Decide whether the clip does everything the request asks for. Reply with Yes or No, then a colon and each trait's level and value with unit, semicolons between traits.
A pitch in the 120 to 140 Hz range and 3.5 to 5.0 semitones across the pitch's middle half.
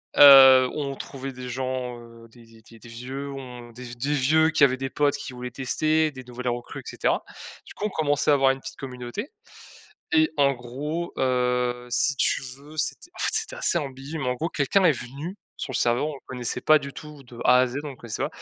No: low, 135 Hz; average, 2.9 semitones